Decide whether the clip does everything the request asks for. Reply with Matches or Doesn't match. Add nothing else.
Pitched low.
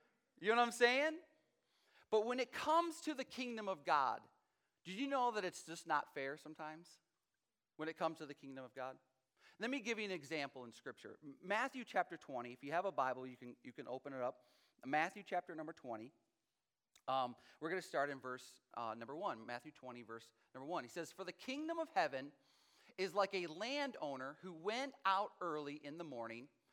Doesn't match